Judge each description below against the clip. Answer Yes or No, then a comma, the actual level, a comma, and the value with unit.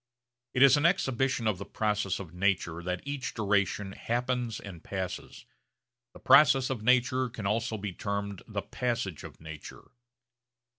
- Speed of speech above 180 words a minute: No, average, 150 wpm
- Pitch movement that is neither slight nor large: Yes, average, 4.4 semitones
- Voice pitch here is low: Yes, low, 105 Hz